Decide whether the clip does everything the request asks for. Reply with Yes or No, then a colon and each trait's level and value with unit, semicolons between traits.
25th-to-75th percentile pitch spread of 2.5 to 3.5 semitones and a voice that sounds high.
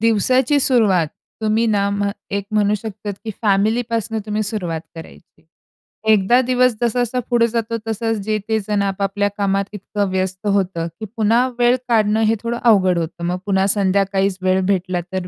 Yes: average, 2.9 semitones; high, 205 Hz